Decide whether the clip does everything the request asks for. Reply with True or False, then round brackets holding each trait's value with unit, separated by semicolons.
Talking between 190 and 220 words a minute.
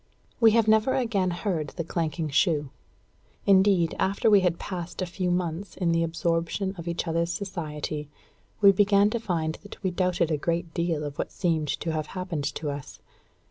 False (180 wpm)